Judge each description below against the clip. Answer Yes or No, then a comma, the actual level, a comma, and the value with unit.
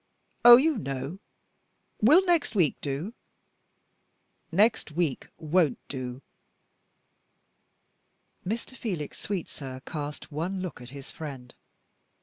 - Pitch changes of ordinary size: No, wide, 7.3 semitones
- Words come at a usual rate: No, slow, 100 wpm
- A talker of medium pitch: Yes, medium, 160 Hz